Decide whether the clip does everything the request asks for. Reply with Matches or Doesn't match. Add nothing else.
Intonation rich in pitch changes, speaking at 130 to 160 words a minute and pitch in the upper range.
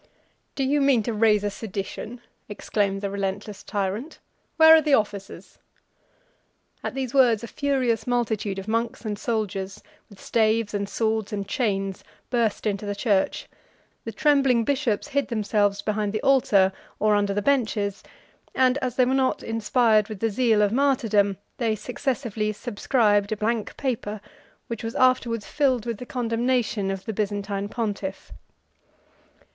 Doesn't match